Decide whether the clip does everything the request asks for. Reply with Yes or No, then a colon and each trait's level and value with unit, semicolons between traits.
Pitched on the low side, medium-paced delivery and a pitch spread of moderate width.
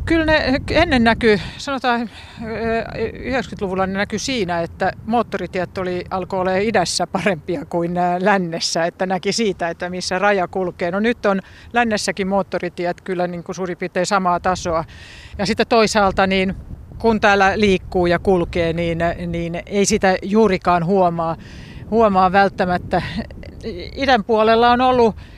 No: high, 190 Hz; average, 135 wpm; average, 3.6 semitones